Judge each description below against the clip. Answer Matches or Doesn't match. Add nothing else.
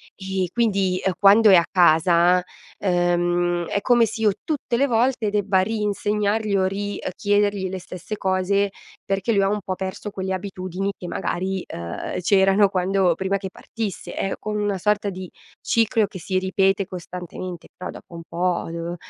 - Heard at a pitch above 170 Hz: Matches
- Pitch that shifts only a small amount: Matches